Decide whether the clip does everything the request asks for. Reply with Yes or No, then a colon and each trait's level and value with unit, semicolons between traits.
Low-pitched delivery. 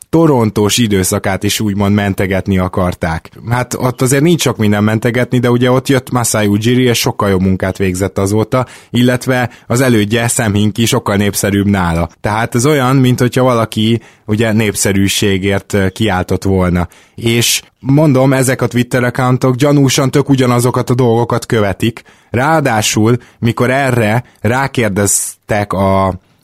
Yes: low, 115 Hz